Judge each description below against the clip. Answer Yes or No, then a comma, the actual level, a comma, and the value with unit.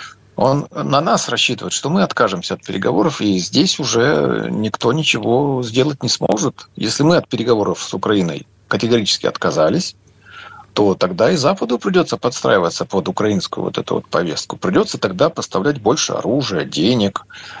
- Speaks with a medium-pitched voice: No, low, 120 Hz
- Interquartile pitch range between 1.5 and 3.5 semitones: No, average, 4.0 semitones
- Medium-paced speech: Yes, average, 145 wpm